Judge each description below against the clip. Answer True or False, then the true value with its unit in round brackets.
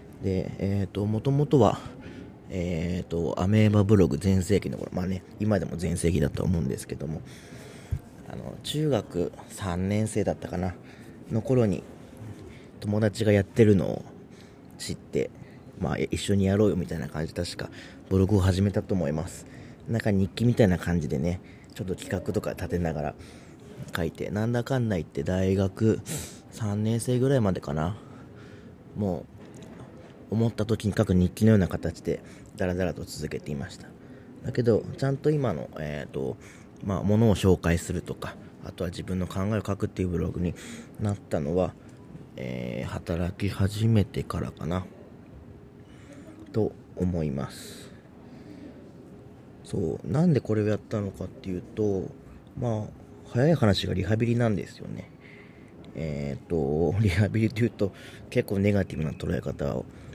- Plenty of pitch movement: False (3.8 semitones)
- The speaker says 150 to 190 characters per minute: False (295 characters per minute)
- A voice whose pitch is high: False (100 Hz)